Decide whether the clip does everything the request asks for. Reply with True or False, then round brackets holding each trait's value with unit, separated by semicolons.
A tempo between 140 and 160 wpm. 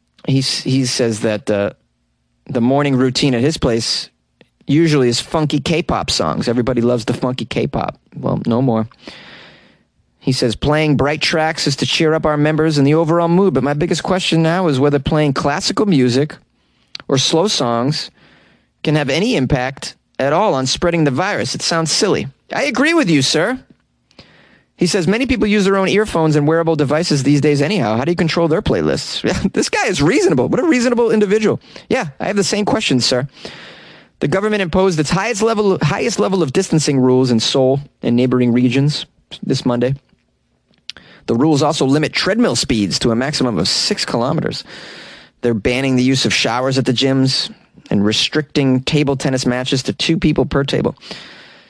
False (180 wpm)